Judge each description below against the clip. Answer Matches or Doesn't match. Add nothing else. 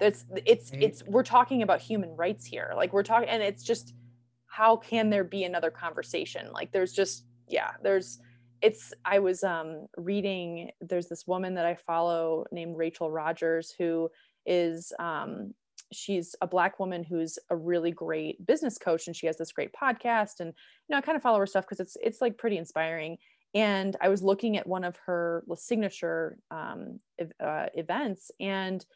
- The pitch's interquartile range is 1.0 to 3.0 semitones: Doesn't match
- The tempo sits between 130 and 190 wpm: Matches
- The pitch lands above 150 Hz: Matches